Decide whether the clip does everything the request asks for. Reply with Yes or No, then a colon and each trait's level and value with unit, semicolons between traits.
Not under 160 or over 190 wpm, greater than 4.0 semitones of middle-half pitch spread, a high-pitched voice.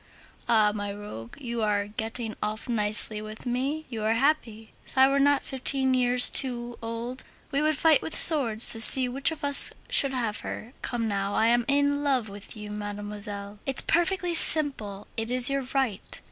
Yes: average, 185 wpm; average, 4.4 semitones; high, 240 Hz